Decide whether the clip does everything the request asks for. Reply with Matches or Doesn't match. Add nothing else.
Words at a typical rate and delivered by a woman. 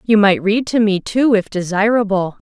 Matches